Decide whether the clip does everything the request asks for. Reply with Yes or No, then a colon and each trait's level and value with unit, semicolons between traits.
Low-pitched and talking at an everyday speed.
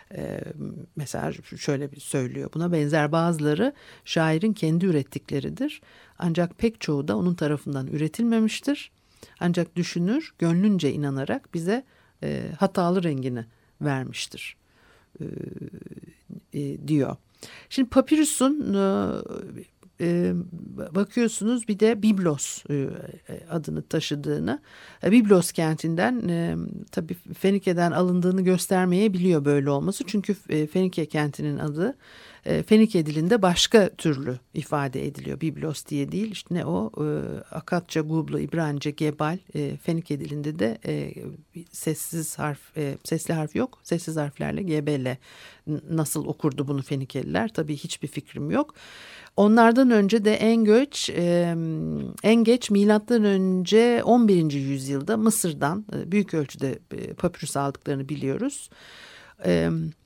No: medium, 170 Hz; average, 105 wpm